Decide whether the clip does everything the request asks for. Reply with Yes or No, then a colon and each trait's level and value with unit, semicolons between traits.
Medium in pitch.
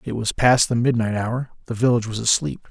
No: low, 120 Hz